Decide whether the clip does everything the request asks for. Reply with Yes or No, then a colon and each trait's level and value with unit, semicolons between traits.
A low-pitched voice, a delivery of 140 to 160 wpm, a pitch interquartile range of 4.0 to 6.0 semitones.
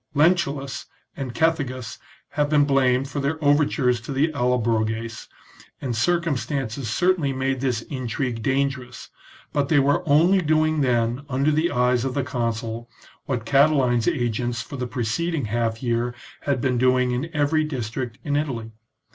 No: low, 130 Hz; average, 150 wpm; average, 3.3 semitones